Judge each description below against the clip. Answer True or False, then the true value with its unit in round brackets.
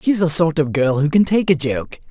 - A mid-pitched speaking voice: True (160 Hz)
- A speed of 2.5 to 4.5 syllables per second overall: False (5.0 syllables/s)